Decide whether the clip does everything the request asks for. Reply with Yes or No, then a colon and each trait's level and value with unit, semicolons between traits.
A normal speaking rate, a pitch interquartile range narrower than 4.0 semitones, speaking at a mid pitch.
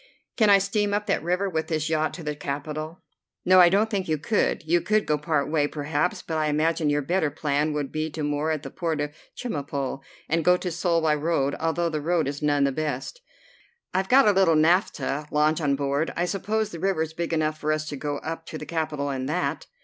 No: fast, 235 wpm; average, 3.0 semitones; medium, 155 Hz